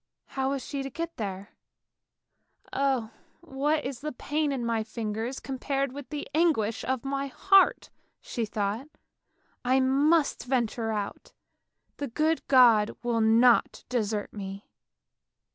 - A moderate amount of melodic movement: Yes, average, 3.9 semitones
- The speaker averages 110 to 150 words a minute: Yes, average, 140 wpm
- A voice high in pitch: Yes, very high, 260 Hz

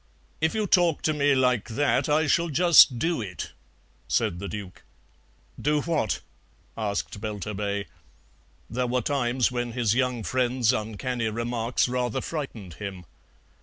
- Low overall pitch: Yes, low, 125 Hz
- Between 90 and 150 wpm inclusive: Yes, slow, 135 wpm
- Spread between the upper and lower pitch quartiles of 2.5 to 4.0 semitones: No, average, 4.9 semitones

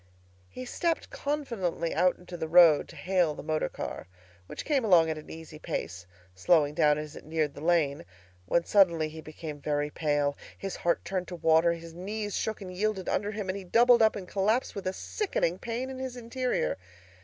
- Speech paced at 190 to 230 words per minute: Yes, average, 200 wpm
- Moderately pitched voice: Yes, medium, 175 Hz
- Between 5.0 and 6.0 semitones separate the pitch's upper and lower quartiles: Yes, wide, 5.4 semitones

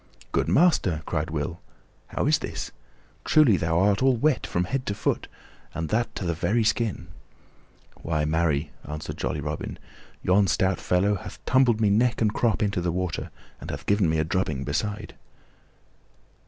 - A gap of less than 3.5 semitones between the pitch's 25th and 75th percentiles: No, average, 5.1 semitones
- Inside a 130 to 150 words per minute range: No, average, 170 wpm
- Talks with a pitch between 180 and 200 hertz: No, very low, 95 Hz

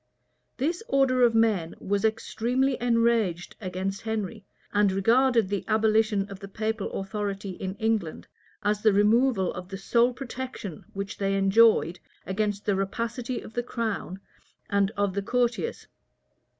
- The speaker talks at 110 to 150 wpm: Yes, average, 140 wpm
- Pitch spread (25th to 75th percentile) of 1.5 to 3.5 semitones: Yes, average, 3.1 semitones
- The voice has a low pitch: No, high, 210 Hz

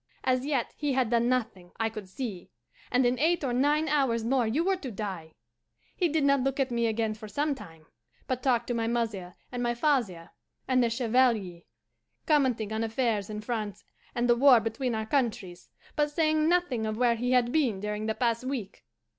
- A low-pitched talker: No, high, 240 Hz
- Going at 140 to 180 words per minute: No, average, 200 wpm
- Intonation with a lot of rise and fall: No, average, 3.6 semitones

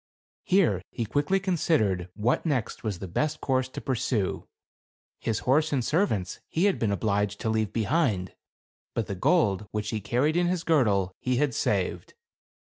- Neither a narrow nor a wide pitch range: No, wide, 7.0 semitones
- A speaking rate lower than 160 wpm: No, average, 165 wpm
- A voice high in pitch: No, low, 120 Hz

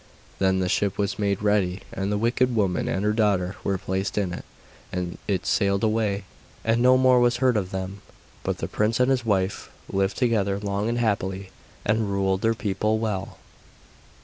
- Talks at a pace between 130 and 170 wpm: No, average, 185 wpm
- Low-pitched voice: Yes, low, 100 Hz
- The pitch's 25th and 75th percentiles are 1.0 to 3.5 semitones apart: Yes, average, 2.7 semitones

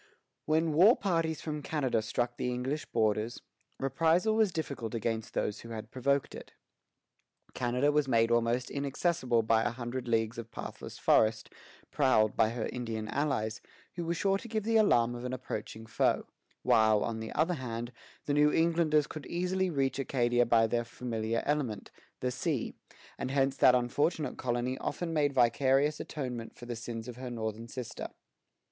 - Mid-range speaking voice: No, low, 125 Hz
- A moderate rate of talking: Yes, average, 165 wpm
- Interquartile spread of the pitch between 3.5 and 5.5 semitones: Yes, average, 4.5 semitones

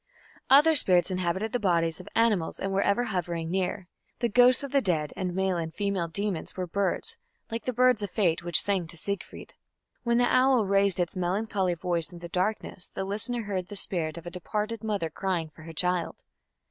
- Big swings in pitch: No, average, 3.6 semitones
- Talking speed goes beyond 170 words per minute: Yes, average, 200 wpm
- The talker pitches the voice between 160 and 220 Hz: Yes, high, 190 Hz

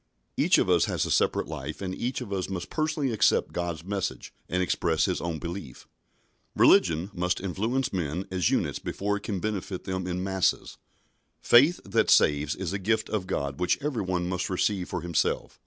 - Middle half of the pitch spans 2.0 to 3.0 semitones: Yes, average, 2.7 semitones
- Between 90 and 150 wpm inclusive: No, average, 190 wpm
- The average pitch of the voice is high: No, very low, 95 Hz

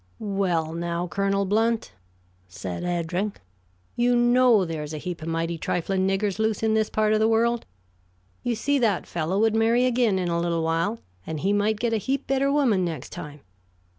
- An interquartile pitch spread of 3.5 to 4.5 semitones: No, average, 4.9 semitones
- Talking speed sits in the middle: Yes, average, 185 wpm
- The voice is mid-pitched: No, high, 200 Hz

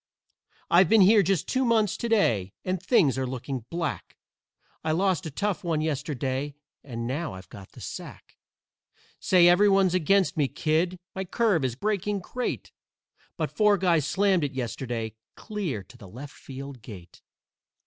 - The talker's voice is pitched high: No, medium, 165 Hz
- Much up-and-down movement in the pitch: Yes, wide, 6.8 semitones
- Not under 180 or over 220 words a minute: No, average, 160 wpm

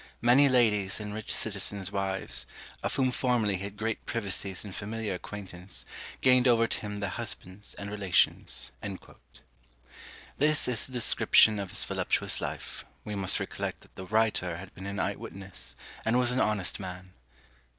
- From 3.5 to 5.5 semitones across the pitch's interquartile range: No, average, 2.9 semitones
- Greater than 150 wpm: Yes, average, 160 wpm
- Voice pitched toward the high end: No, low, 105 Hz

